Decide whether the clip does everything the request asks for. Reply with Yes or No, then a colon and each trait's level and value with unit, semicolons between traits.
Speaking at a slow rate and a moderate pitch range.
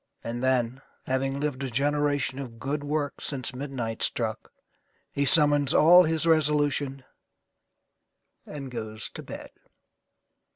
No: slow, 120 wpm; narrow, 2.3 semitones